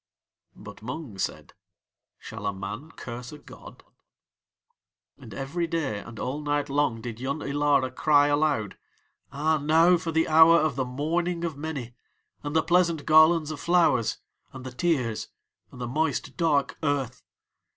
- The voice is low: No, medium, 145 Hz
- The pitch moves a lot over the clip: No, average, 4.1 semitones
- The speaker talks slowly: No, average, 150 wpm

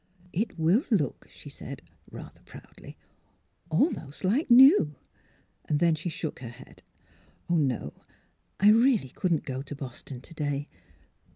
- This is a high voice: No, medium, 160 Hz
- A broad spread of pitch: Yes, wide, 6.3 semitones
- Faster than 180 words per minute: No, average, 145 wpm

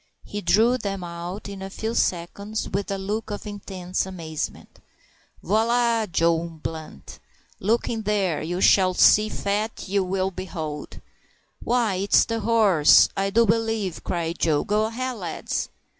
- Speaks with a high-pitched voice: Yes, high, 195 Hz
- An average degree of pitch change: Yes, average, 3.7 semitones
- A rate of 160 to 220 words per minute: No, average, 150 wpm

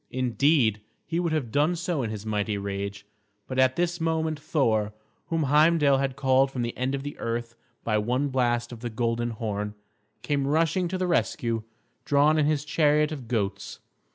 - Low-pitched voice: Yes, low, 130 Hz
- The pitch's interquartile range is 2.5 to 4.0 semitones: No, average, 4.9 semitones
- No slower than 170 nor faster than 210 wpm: Yes, average, 180 wpm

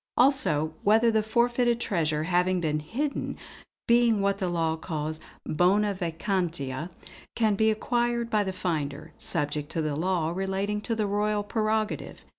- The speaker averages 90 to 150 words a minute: Yes, average, 145 wpm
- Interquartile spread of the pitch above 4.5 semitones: Yes, average, 5.2 semitones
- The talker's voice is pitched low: No, high, 195 Hz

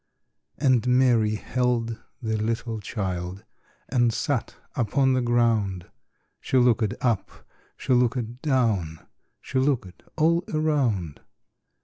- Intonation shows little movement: No, average, 3.2 semitones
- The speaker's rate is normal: No, slow, 105 wpm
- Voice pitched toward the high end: No, low, 120 Hz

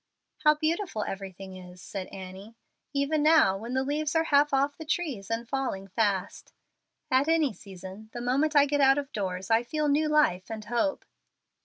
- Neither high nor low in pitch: No, very high, 255 Hz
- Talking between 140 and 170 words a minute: No, average, 180 wpm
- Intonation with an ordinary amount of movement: No, wide, 7.1 semitones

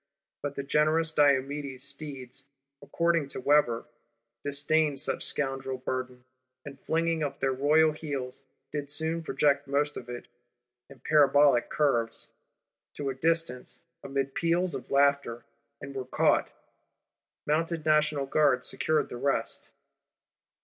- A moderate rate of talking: No, slow, 125 wpm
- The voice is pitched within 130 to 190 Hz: Yes, medium, 140 Hz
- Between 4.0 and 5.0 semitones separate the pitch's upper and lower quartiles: No, narrow, 2.4 semitones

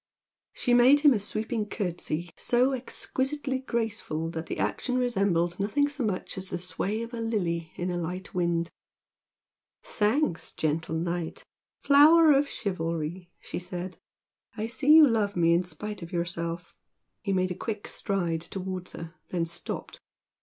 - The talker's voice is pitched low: No, high, 190 Hz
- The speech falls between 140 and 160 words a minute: Yes, average, 155 wpm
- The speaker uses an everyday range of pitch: No, wide, 5.7 semitones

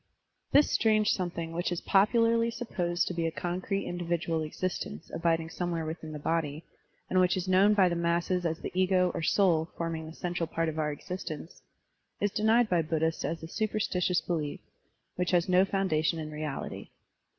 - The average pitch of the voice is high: No, medium, 175 Hz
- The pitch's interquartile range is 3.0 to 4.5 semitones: No, narrow, 2.5 semitones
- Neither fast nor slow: Yes, average, 175 wpm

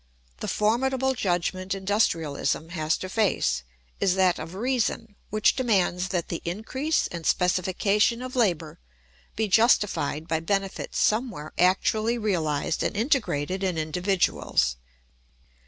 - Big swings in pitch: No, average, 4.5 semitones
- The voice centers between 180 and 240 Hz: Yes, high, 190 Hz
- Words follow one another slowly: Yes, slow, 120 wpm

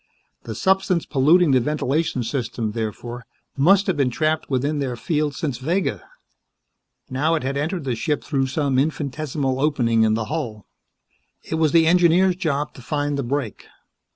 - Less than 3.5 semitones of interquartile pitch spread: No, average, 3.8 semitones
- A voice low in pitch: No, medium, 145 Hz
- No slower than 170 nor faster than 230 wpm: No, average, 160 wpm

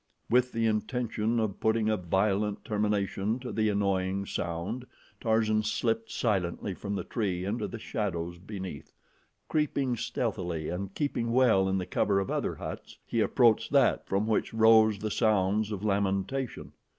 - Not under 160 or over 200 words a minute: No, average, 150 wpm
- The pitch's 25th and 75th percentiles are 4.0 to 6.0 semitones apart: No, average, 2.8 semitones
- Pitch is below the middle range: Yes, low, 105 Hz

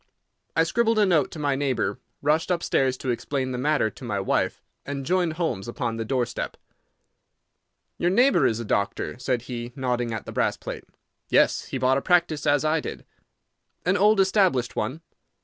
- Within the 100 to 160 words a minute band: No, average, 185 wpm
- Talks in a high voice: No, medium, 140 Hz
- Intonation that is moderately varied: No, wide, 5.7 semitones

